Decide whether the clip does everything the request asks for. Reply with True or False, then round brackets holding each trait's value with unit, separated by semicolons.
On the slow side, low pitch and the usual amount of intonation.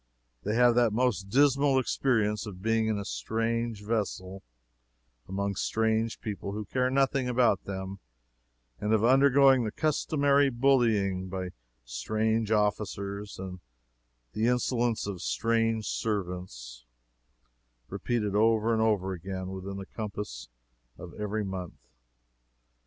True (120 wpm; 110 Hz; 3.4 semitones)